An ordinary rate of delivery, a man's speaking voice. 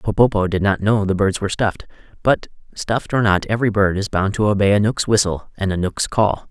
No: fast, 230 wpm; male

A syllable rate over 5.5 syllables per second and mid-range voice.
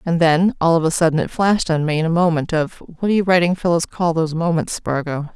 Yes: 6.0 syllables/s; medium, 165 Hz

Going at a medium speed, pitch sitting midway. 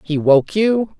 Yes: average, 180 wpm; medium, 180 Hz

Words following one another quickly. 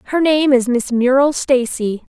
No: average, 165 wpm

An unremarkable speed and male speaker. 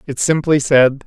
Yes: average, 170 wpm; male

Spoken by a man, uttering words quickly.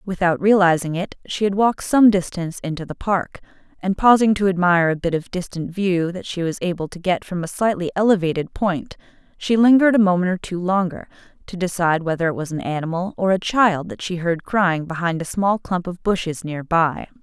No: female; fast, 210 wpm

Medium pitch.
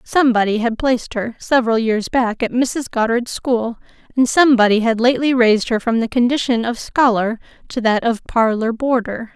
No: high, 235 Hz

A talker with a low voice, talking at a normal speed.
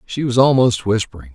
Yes: low, 120 Hz; average, 180 wpm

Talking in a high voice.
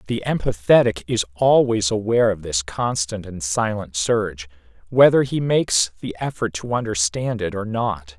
No: low, 105 Hz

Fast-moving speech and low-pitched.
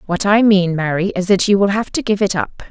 No: fast, 290 wpm; high, 195 Hz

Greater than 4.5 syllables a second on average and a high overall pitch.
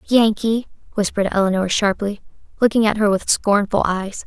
Yes: 5.3 syllables/s; high, 205 Hz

